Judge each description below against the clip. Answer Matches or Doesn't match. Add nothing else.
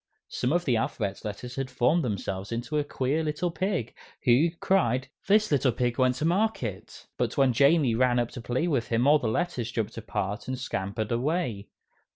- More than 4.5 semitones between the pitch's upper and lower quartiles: Matches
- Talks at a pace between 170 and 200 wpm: Matches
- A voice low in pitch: Matches